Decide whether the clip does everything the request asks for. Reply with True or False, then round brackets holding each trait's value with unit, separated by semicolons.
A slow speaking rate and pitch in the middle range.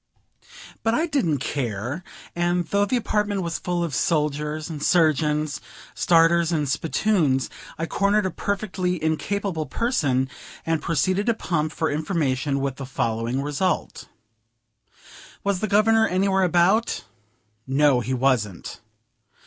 True (125 wpm; 165 Hz)